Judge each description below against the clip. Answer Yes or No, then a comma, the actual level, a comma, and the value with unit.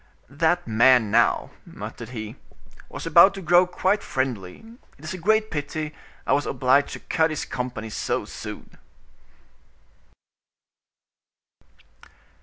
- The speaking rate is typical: No, slow, 120 wpm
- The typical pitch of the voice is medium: Yes, medium, 145 Hz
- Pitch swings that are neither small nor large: No, wide, 6.3 semitones